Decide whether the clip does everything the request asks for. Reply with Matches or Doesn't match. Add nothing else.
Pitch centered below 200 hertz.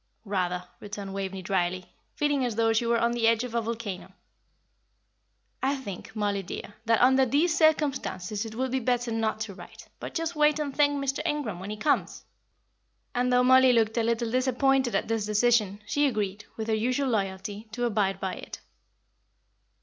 Doesn't match